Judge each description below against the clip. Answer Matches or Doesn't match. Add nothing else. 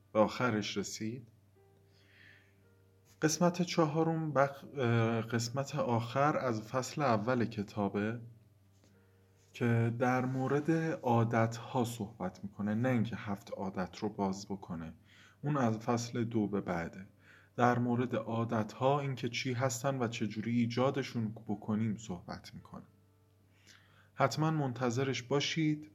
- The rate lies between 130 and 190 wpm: Doesn't match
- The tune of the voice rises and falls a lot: Doesn't match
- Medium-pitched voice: Doesn't match